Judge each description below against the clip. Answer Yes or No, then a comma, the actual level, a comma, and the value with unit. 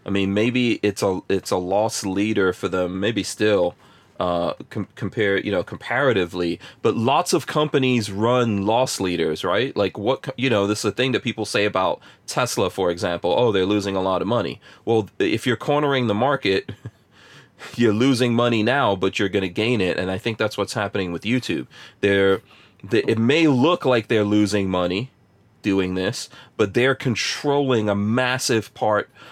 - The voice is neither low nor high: No, low, 105 Hz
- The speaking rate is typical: Yes, average, 180 wpm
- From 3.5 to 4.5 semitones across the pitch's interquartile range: Yes, average, 4.0 semitones